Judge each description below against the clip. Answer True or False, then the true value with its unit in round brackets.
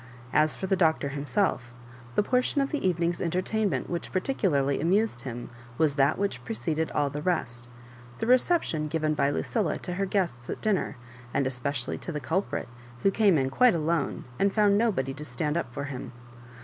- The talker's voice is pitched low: False (160 Hz)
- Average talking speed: True (190 wpm)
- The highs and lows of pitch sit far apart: True (6.1 semitones)